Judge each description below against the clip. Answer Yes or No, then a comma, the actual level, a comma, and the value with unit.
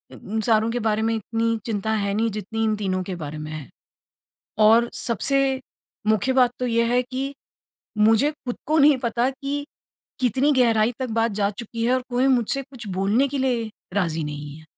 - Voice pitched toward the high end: Yes, high, 230 Hz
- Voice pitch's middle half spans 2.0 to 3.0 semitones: No, average, 3.5 semitones